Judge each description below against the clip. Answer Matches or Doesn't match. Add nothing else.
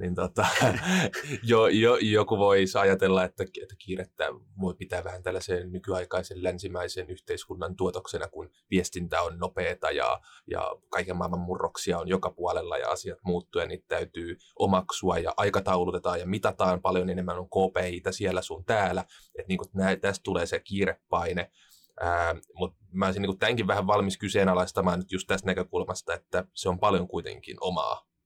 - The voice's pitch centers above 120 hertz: Doesn't match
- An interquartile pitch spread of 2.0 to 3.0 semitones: Doesn't match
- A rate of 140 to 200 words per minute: Matches